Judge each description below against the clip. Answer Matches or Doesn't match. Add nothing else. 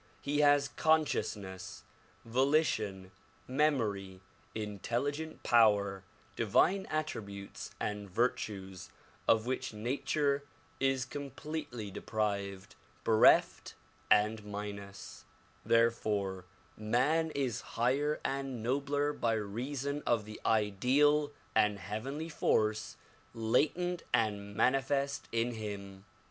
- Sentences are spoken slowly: Matches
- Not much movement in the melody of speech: Doesn't match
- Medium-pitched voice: Doesn't match